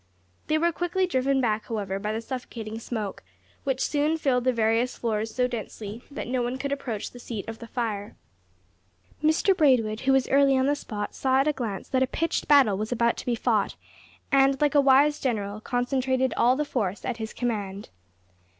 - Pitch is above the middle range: Yes, very high, 250 Hz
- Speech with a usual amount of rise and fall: Yes, average, 3.7 semitones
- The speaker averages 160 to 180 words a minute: No, average, 195 wpm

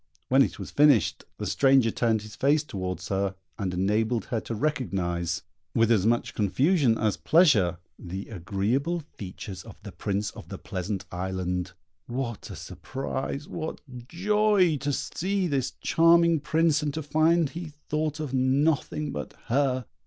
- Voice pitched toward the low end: Yes, low, 130 Hz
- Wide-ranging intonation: Yes, wide, 7.5 semitones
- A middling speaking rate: Yes, average, 150 wpm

